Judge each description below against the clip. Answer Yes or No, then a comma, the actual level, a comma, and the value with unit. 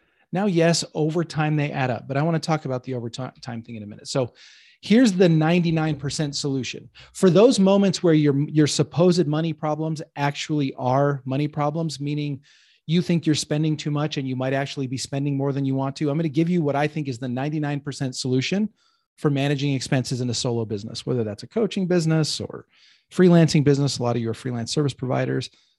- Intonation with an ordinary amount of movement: Yes, average, 3.4 semitones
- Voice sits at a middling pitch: Yes, medium, 145 Hz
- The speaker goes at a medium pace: No, fast, 210 wpm